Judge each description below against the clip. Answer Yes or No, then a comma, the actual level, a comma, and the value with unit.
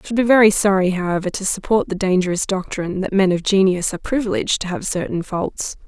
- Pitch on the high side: Yes, high, 195 Hz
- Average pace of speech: No, fast, 215 wpm